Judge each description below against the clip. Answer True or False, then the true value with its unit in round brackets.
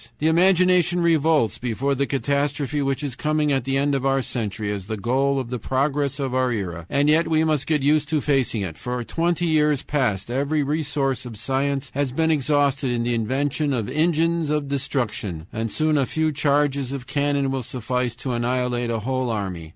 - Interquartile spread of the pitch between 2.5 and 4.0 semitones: True (3.4 semitones)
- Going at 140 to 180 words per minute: False (195 wpm)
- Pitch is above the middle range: False (135 Hz)